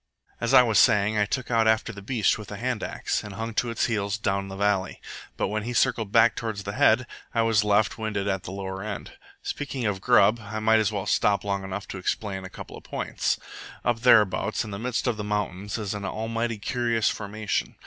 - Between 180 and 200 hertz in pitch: No, low, 105 Hz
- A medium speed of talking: No, fast, 225 wpm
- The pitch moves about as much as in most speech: No, narrow, 2.2 semitones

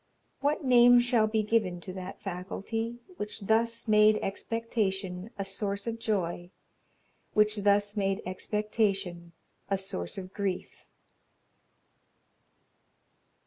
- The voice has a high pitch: Yes, high, 205 Hz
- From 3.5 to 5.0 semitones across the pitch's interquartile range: No, average, 2.7 semitones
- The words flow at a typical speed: No, slow, 105 wpm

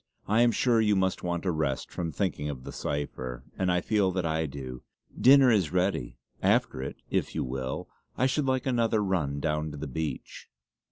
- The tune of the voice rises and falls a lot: Yes, wide, 6.7 semitones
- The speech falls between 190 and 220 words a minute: Yes, average, 200 wpm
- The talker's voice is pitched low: Yes, very low, 90 Hz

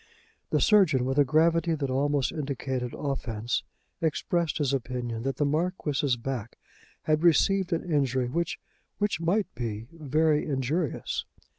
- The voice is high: No, medium, 145 Hz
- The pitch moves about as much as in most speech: Yes, average, 4.2 semitones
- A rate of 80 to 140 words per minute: Yes, slow, 135 wpm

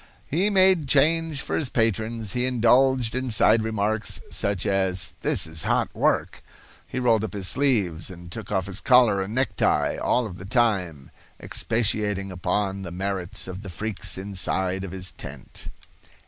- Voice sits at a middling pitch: No, low, 105 Hz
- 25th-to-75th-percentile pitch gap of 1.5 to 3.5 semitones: No, average, 4.5 semitones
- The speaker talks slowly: No, average, 160 wpm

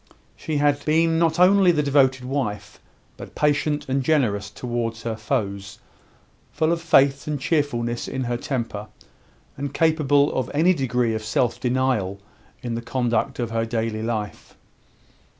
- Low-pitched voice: Yes, low, 130 Hz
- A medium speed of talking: Yes, average, 150 wpm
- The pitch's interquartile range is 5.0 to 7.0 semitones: No, average, 4.3 semitones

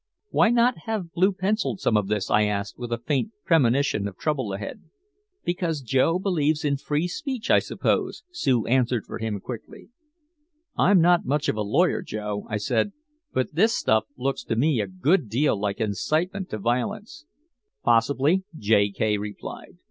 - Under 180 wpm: Yes, average, 170 wpm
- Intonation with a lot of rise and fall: Yes, wide, 8.4 semitones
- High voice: No, low, 130 Hz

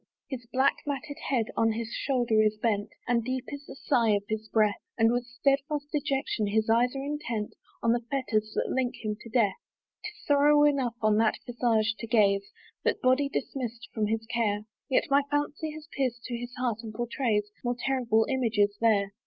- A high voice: Yes, high, 235 Hz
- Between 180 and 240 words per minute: Yes, average, 190 wpm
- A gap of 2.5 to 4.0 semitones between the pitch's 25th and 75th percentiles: Yes, average, 3.7 semitones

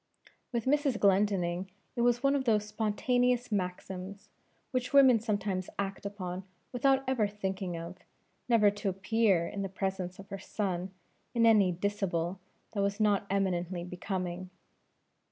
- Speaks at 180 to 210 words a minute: No, average, 140 wpm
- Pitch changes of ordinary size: Yes, average, 3.5 semitones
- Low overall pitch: No, high, 200 Hz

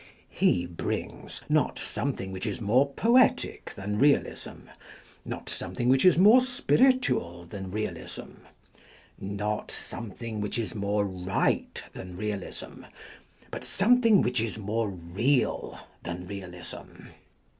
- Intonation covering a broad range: Yes, wide, 6.2 semitones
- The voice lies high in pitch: No, low, 105 Hz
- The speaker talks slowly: Yes, slow, 125 wpm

